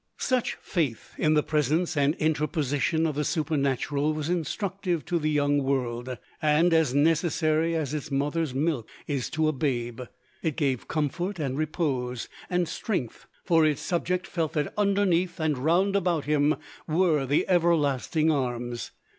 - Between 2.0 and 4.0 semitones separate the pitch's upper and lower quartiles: Yes, average, 3.1 semitones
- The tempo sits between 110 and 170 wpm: Yes, average, 150 wpm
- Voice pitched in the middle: Yes, medium, 155 Hz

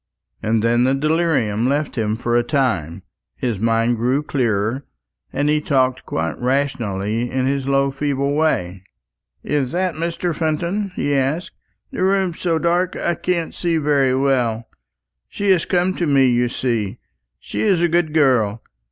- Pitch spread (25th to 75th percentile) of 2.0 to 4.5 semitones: No, average, 5.3 semitones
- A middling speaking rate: Yes, average, 155 wpm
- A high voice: No, low, 135 Hz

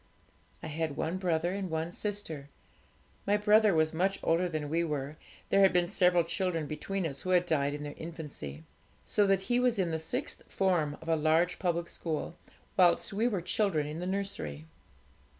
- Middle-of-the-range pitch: Yes, medium, 170 Hz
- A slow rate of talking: No, average, 185 wpm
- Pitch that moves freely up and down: No, average, 3.5 semitones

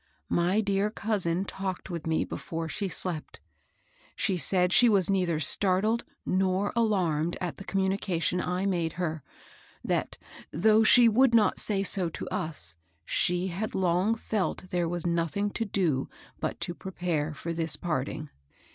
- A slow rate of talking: No, average, 150 wpm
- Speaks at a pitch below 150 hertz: No, medium, 185 Hz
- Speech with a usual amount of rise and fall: Yes, average, 3.0 semitones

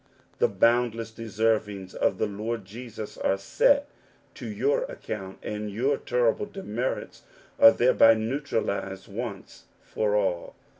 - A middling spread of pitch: Yes, average, 3.2 semitones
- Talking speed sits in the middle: No, slow, 120 wpm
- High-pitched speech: No, low, 110 Hz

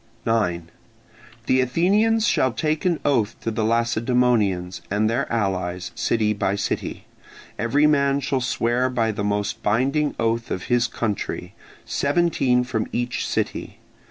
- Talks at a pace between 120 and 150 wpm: Yes, slow, 135 wpm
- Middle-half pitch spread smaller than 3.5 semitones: No, average, 4.3 semitones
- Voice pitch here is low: Yes, low, 120 Hz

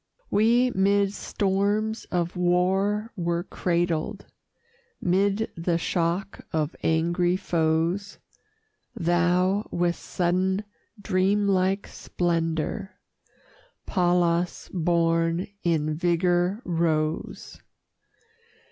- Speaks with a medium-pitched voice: Yes, medium, 180 Hz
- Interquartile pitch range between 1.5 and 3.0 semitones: Yes, narrow, 2.6 semitones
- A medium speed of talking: No, slow, 75 wpm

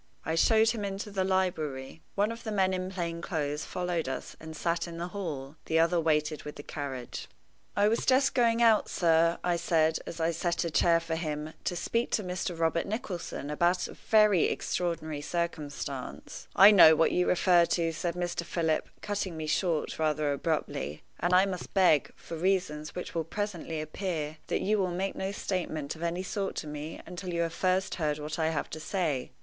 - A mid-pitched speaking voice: Yes, medium, 170 Hz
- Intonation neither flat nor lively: Yes, average, 3.1 semitones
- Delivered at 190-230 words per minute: Yes, average, 200 wpm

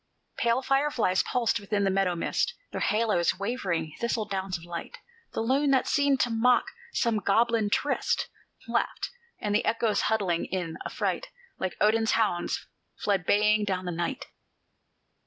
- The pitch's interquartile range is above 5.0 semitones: No, average, 3.9 semitones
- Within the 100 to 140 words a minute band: No, average, 150 wpm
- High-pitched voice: Yes, high, 210 Hz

